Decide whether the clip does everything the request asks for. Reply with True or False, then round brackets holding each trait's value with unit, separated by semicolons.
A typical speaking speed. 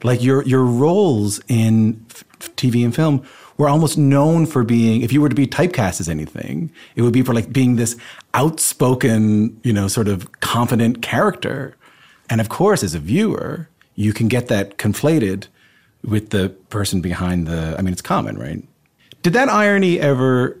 True (180 wpm)